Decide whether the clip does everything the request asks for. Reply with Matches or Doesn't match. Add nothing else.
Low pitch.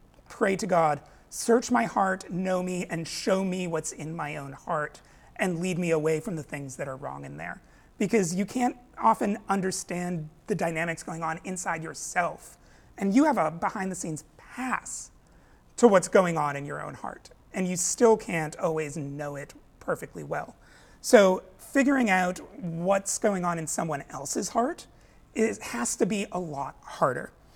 Doesn't match